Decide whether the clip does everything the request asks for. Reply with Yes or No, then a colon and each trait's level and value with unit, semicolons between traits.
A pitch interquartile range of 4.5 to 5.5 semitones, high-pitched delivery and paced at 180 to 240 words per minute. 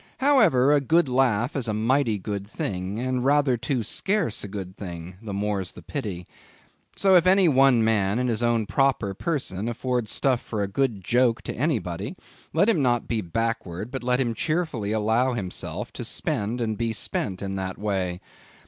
No: average, 4.8 semitones; low, 115 Hz; average, 185 wpm